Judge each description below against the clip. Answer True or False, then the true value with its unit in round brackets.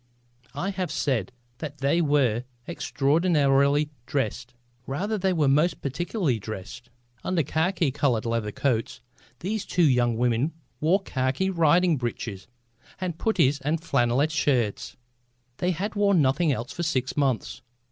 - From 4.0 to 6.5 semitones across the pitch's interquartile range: True (5.2 semitones)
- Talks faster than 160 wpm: False (135 wpm)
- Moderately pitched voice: True (145 Hz)